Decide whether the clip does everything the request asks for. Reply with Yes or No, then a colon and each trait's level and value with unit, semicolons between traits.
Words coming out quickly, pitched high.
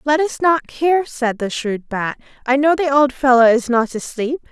Yes: fast, 215 wpm; very high, 265 Hz